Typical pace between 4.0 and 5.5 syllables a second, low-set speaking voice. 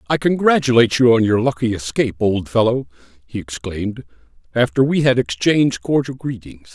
No: 5.7 syllables/s; low, 115 Hz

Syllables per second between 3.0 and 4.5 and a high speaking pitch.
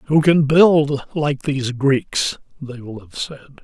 No: 3.5 syllables/s; medium, 140 Hz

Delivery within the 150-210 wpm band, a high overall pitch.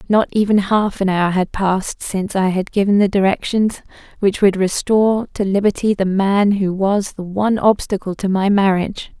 Yes: average, 185 wpm; high, 195 Hz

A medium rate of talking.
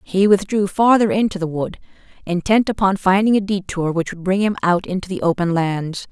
Yes: average, 195 wpm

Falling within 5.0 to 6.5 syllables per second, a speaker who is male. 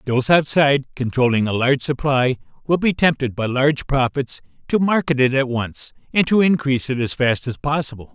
Yes: 5.5 syllables/s; male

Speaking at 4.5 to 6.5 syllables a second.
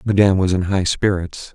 Yes: 5.5 syllables/s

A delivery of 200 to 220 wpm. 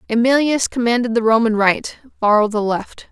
No: average, 155 wpm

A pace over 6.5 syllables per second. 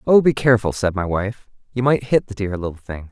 No: 5.8 syllables/s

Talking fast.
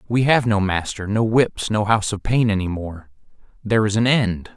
Yes: fast, 210 wpm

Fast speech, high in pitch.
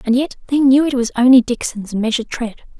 Yes: fast, 215 wpm; very high, 250 Hz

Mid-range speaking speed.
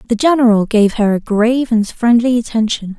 Yes: average, 180 wpm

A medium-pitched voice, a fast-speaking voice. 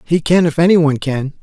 Yes: medium, 155 Hz; fast, 255 wpm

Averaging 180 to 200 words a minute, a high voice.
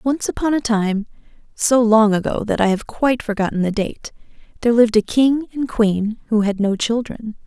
Yes: average, 195 wpm; high, 225 Hz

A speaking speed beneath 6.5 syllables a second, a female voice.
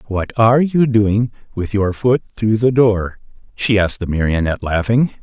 No: 5.0 syllables/s; male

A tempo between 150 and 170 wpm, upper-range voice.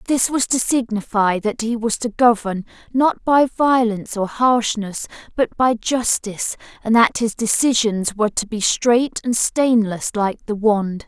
Yes: average, 165 wpm; high, 225 Hz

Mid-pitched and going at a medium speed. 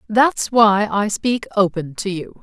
No: high, 210 Hz; average, 175 wpm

